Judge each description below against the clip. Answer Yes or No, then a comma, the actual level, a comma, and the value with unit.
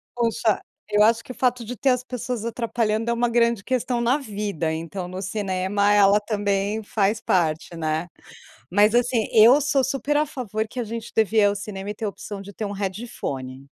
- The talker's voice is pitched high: Yes, high, 215 Hz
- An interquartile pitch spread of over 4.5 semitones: No, average, 3.2 semitones